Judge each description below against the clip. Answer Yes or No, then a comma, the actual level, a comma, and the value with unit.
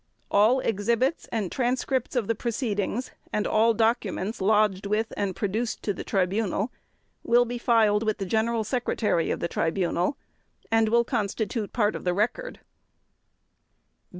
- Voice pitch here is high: Yes, high, 220 Hz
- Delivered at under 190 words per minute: Yes, average, 145 wpm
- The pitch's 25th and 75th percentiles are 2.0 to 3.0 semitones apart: Yes, average, 2.7 semitones